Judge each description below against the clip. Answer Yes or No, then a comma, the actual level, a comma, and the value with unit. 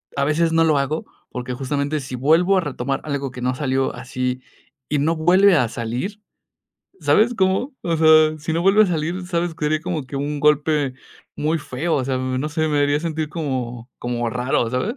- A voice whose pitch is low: No, medium, 150 Hz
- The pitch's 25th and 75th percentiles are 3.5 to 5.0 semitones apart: Yes, average, 4.1 semitones